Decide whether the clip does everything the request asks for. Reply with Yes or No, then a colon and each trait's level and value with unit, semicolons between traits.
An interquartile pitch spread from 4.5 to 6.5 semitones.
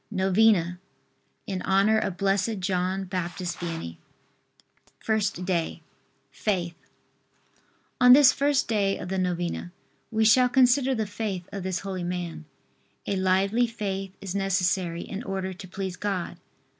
No: average, 3.0 semitones